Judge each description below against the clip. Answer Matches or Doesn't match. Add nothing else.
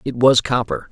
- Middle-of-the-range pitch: Doesn't match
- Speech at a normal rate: Matches